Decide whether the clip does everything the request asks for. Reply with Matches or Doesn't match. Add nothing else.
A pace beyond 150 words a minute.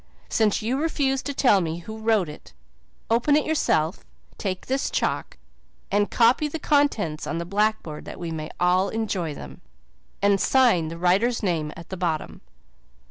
Matches